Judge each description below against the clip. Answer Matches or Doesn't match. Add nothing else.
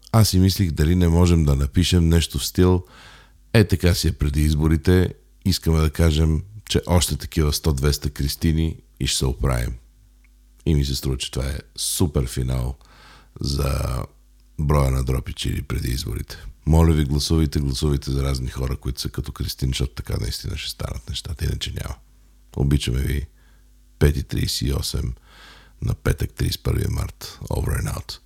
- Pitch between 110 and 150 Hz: Doesn't match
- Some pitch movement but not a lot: Matches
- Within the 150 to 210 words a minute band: Matches